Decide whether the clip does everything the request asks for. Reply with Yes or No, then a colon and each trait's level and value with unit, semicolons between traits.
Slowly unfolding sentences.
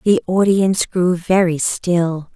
Yes: slow, 125 wpm